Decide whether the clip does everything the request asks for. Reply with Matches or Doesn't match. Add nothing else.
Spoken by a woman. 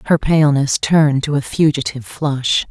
Matches